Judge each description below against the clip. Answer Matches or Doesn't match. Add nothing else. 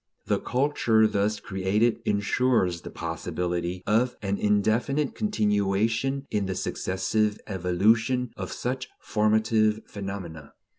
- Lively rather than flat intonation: Doesn't match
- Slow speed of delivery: Matches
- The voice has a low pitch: Matches